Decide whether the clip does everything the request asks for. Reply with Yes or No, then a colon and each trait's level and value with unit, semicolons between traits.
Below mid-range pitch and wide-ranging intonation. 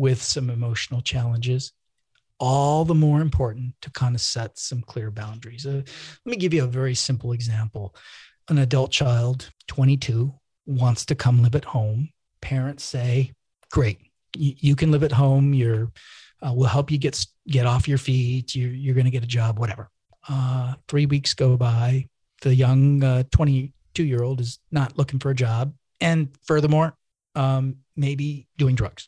No: low, 130 Hz; average, 2.7 semitones